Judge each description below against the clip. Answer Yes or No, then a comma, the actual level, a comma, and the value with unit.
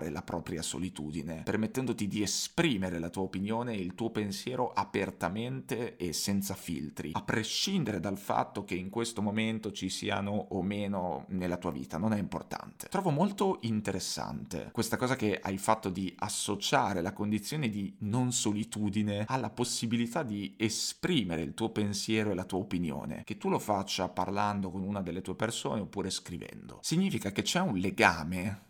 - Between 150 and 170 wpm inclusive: Yes, average, 165 wpm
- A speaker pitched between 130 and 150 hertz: No, low, 105 Hz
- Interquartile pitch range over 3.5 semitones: No, average, 2.9 semitones